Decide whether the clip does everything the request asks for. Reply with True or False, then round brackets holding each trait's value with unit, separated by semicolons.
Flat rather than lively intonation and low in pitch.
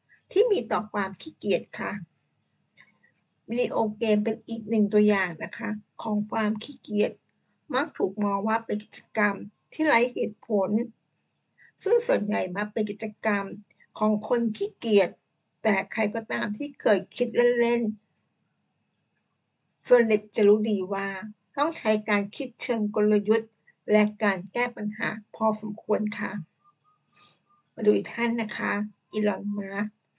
False (1.9 semitones; 215 Hz)